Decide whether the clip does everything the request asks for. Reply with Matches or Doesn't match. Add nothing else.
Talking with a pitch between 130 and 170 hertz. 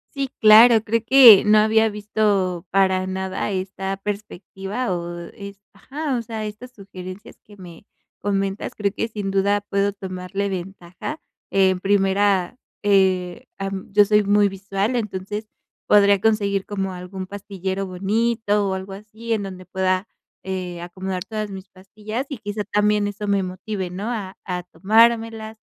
Doesn't match